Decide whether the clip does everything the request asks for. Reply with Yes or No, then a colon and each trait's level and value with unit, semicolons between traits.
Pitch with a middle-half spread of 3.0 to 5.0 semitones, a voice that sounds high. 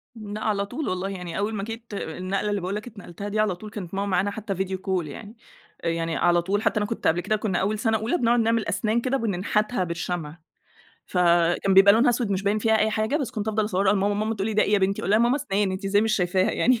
No: narrow, 2.6 semitones; high, 205 Hz